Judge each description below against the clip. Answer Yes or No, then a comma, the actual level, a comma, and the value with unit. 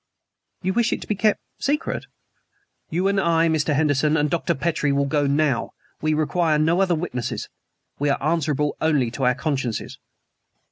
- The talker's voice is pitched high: No, medium, 155 Hz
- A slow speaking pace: No, average, 170 wpm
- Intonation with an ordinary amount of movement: Yes, average, 3.2 semitones